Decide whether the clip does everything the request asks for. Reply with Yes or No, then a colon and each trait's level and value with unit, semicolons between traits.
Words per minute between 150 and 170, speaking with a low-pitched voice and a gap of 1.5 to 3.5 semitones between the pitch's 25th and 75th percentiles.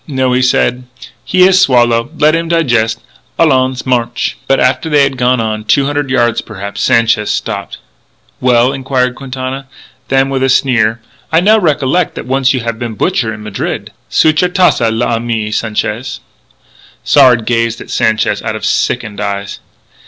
Yes: average, 165 wpm; low, 125 Hz; average, 2.9 semitones